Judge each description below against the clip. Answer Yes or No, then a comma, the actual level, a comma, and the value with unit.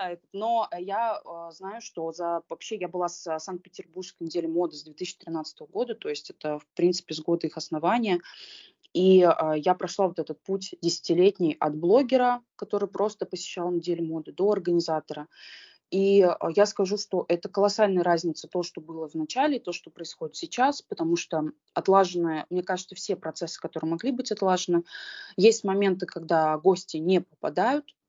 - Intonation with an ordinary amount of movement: Yes, average, 3.5 semitones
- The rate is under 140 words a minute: No, average, 155 wpm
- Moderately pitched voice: Yes, medium, 180 Hz